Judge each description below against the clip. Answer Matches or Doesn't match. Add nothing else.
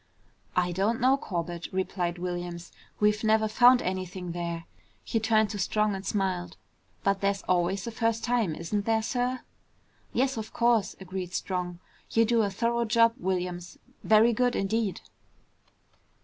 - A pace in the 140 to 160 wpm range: Matches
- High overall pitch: Matches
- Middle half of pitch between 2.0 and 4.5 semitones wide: Matches